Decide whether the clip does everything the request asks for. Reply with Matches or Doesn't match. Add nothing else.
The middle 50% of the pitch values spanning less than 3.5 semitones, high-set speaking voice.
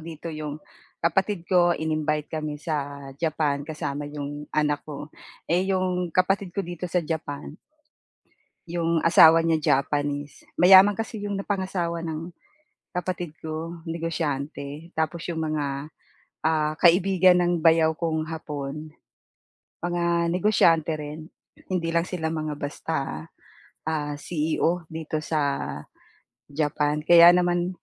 Doesn't match